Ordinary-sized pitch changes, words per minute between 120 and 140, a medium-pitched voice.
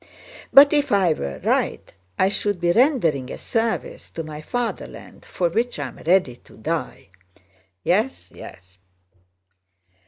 No: wide, 7.3 semitones; slow, 135 wpm; medium, 175 Hz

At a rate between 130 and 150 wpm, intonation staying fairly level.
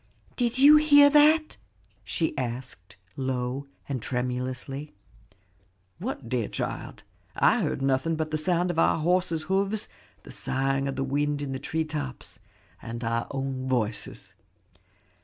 No: average, 140 wpm; average, 5.3 semitones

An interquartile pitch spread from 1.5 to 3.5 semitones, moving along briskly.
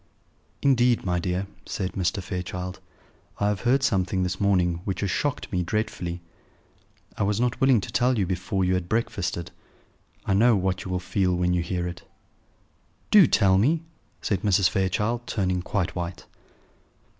No: average, 2.9 semitones; average, 165 wpm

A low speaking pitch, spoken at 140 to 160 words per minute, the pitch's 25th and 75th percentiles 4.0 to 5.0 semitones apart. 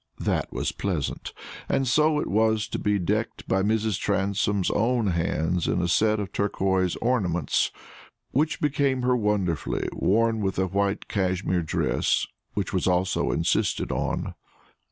No: low, 100 Hz; average, 145 wpm; average, 3.3 semitones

